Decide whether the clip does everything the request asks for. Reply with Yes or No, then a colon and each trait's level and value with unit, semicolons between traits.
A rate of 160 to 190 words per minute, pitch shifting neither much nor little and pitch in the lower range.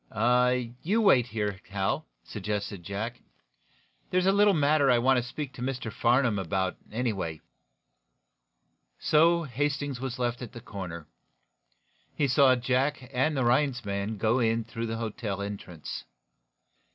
No: average, 140 wpm; average, 4.7 semitones; low, 120 Hz